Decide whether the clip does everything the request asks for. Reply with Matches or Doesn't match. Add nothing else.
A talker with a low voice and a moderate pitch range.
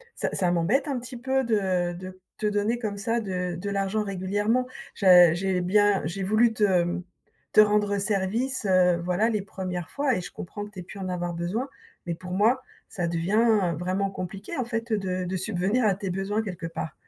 Doesn't match